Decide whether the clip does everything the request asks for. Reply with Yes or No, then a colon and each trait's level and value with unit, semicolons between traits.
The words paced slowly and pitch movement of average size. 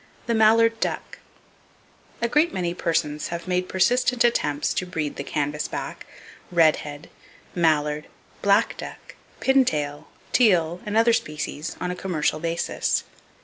No: slow, 120 wpm; wide, 6.7 semitones